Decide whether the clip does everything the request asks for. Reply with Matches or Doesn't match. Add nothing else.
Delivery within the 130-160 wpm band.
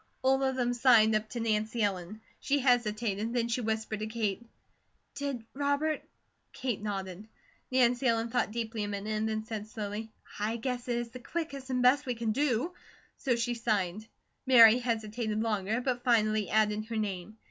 Doesn't match